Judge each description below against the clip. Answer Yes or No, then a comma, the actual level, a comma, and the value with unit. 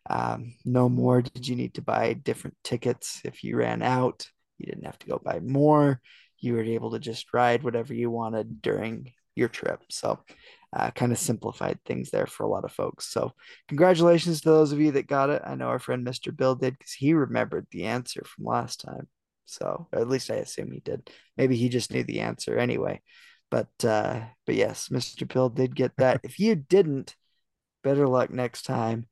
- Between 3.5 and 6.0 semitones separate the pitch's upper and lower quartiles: No, narrow, 2.6 semitones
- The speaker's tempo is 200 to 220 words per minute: Yes, fast, 205 wpm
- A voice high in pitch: No, low, 125 Hz